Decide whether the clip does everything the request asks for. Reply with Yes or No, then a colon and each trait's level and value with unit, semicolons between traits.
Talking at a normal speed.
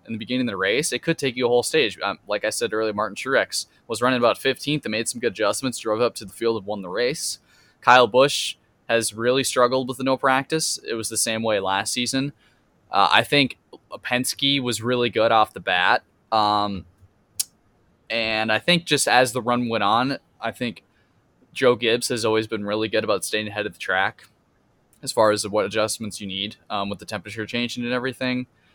No: fast, 215 wpm